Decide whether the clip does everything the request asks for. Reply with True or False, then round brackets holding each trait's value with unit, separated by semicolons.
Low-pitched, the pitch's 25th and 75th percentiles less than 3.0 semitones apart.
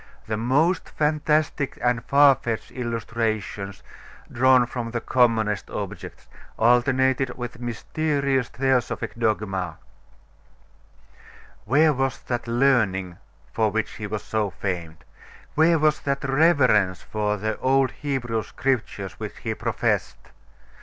False (120 Hz; 3.9 semitones)